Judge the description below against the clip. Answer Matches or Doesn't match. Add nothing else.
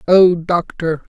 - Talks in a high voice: Doesn't match